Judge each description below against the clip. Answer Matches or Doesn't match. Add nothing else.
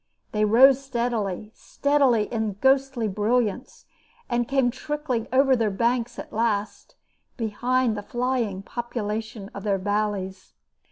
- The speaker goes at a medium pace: Doesn't match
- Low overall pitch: Doesn't match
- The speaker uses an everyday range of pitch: Matches